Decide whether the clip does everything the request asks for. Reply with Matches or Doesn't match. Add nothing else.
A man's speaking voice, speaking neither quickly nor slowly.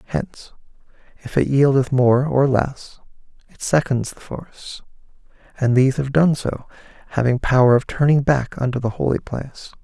Matches